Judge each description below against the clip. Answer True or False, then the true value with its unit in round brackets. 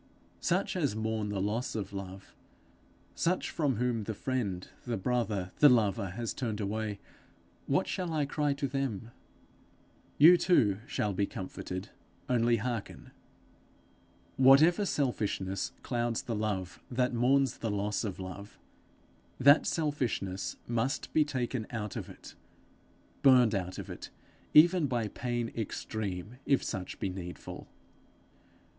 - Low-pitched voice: True (115 Hz)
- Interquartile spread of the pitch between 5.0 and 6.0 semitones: False (4.6 semitones)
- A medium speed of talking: False (130 wpm)